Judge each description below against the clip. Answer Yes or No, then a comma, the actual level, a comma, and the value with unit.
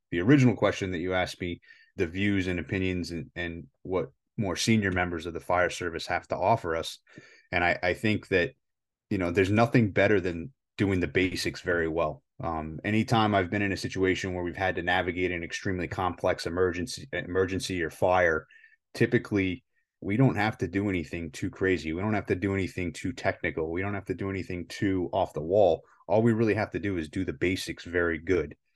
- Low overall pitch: Yes, very low, 95 Hz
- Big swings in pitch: No, average, 2.8 semitones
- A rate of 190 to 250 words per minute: Yes, fast, 205 wpm